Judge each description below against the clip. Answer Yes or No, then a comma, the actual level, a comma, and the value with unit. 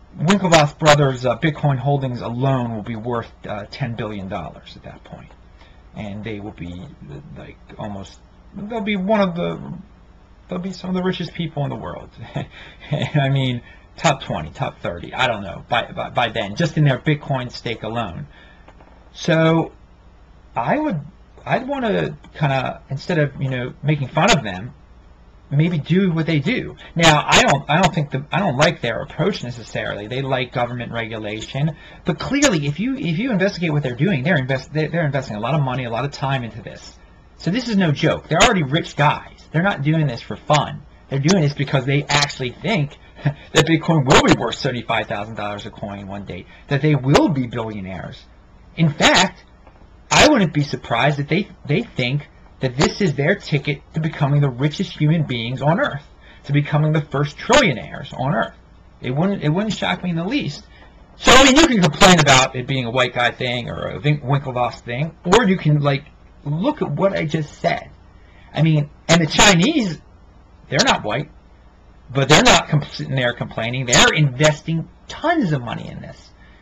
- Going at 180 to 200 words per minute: Yes, average, 190 wpm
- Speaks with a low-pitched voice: No, medium, 145 Hz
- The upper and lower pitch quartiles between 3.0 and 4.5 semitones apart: No, average, 5.3 semitones